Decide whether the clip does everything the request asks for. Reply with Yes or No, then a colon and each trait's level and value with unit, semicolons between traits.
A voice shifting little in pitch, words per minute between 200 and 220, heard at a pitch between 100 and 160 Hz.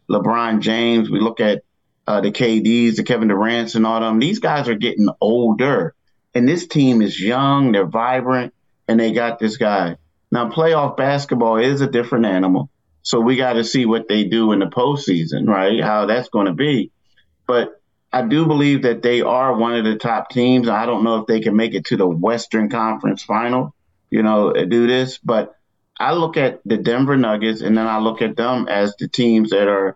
Yes: narrow, 2.2 semitones; fast, 205 wpm; low, 115 Hz